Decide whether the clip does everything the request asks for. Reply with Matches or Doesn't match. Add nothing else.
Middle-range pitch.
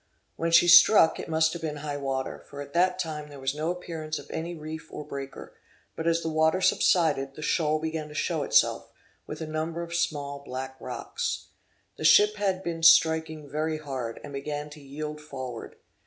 Matches